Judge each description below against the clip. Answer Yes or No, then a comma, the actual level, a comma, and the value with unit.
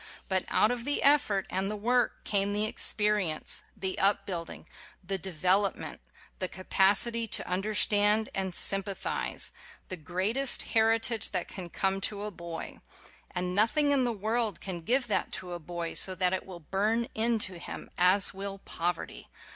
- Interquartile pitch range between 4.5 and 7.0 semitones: No, average, 3.1 semitones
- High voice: Yes, high, 195 Hz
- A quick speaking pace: No, average, 160 wpm